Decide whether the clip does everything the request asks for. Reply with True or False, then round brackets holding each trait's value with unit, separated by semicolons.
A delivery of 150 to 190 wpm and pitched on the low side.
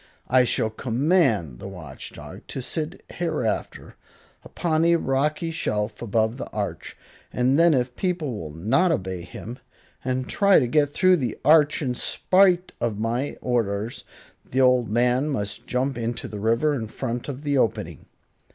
True (160 wpm; 125 Hz)